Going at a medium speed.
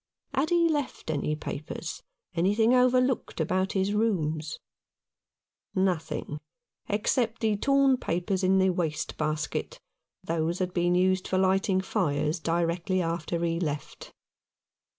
No: slow, 125 wpm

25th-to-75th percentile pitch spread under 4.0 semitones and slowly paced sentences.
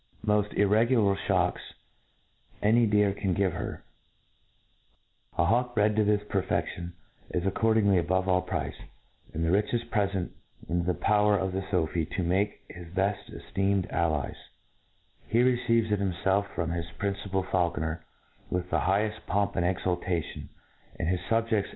No: average, 2.8 semitones; average, 145 wpm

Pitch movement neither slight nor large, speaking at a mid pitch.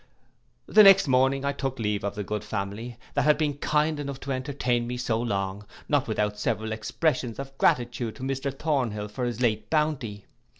No: average, 4.4 semitones; low, 125 Hz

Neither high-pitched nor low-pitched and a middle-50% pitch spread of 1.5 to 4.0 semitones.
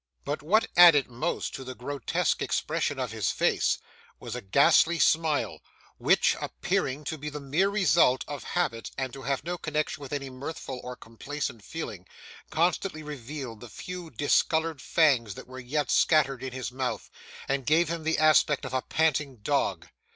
Yes: medium, 145 Hz; average, 3.6 semitones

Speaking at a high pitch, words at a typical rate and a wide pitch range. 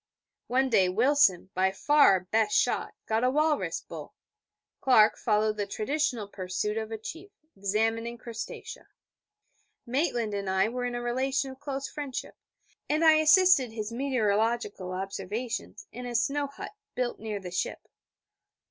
No: high, 230 Hz; average, 150 wpm; average, 4.3 semitones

